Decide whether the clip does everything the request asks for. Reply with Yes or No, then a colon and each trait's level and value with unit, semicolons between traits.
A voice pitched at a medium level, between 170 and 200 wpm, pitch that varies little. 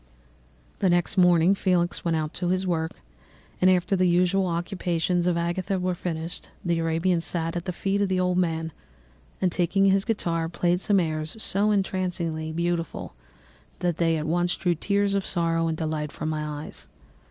Yes: medium, 175 Hz; average, 175 wpm; narrow, 2.0 semitones